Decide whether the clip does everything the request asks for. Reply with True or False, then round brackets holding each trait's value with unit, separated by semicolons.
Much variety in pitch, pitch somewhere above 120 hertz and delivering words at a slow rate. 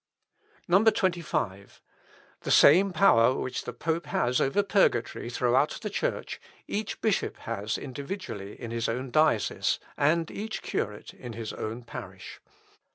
True (8.2 semitones; 135 Hz; 130 wpm)